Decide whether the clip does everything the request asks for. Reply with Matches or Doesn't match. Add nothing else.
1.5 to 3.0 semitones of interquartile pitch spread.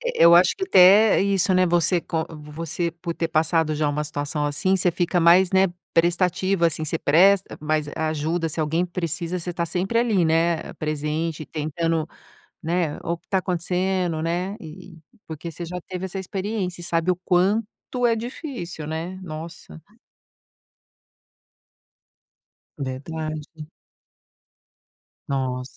Matches